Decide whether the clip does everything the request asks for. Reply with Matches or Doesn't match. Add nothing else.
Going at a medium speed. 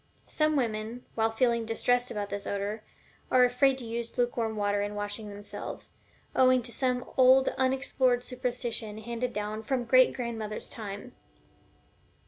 Matches